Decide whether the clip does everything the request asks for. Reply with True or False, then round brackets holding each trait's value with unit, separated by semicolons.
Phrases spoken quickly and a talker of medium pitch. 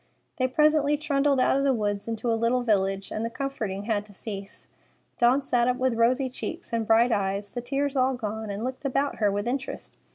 False (215 wpm; 240 Hz)